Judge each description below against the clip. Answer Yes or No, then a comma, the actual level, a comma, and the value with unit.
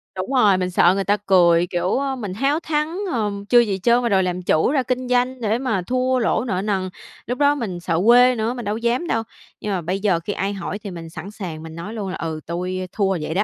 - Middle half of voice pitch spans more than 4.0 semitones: Yes, average, 5.2 semitones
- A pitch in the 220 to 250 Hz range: No, high, 205 Hz